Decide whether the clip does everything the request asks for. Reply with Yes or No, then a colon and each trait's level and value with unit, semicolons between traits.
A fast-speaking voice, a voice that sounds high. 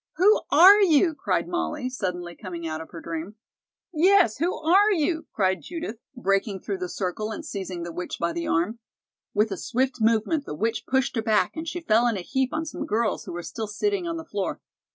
Yes: fast, 215 wpm; high, 225 Hz